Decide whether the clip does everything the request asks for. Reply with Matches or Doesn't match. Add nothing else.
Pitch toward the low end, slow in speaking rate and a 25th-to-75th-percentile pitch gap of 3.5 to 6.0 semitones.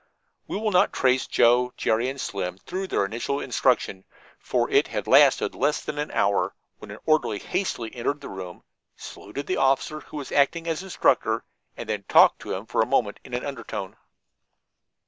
Doesn't match